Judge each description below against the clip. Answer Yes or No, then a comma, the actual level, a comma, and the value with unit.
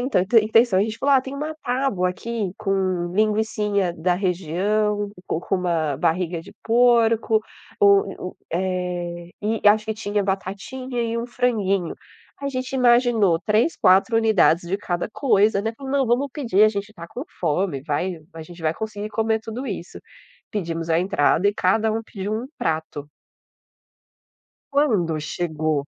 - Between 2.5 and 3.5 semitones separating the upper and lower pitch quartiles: No, average, 4.2 semitones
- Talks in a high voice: Yes, high, 205 Hz